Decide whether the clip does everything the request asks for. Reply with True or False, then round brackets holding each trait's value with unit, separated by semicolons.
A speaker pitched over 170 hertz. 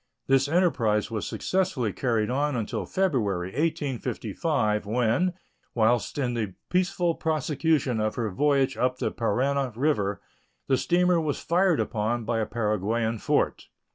False (125 Hz)